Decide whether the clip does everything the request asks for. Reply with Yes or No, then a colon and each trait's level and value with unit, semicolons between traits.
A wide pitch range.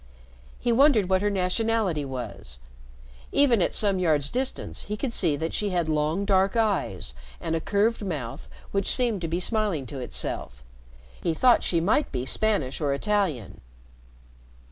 Yes: wide, 6.2 semitones